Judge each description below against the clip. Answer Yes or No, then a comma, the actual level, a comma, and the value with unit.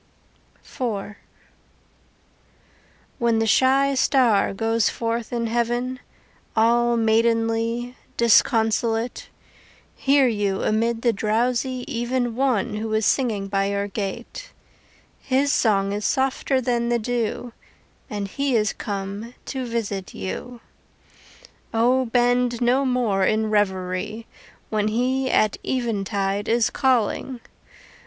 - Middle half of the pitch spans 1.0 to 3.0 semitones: Yes, average, 2.7 semitones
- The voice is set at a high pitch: Yes, high, 230 Hz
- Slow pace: Yes, slow, 110 wpm